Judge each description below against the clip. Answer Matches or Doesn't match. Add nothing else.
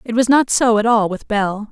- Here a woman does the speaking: Matches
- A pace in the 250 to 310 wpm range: Matches